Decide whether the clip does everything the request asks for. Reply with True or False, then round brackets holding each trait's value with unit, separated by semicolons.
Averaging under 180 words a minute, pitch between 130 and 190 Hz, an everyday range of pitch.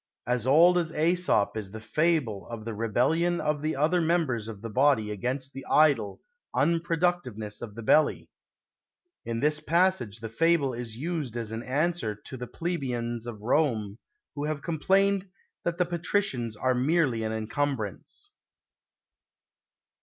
False (145 wpm; 135 Hz; 6.5 semitones)